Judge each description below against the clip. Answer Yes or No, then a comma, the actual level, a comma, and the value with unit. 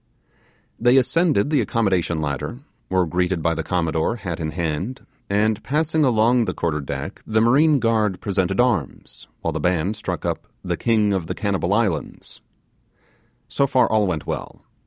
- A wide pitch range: Yes, wide, 5.8 semitones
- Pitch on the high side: No, low, 100 Hz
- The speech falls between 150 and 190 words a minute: Yes, average, 160 wpm